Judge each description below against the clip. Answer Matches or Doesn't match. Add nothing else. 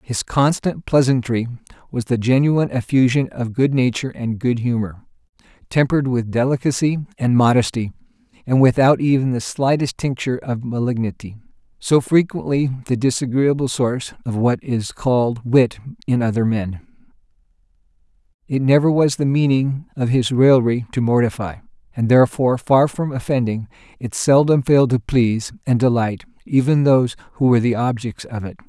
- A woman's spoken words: Doesn't match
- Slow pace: Doesn't match